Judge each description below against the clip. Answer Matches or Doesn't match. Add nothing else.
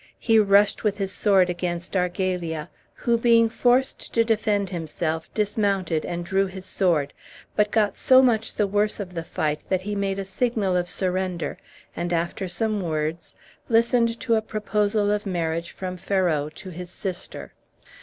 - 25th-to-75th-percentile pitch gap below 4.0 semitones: Matches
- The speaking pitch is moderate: Doesn't match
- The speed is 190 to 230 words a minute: Doesn't match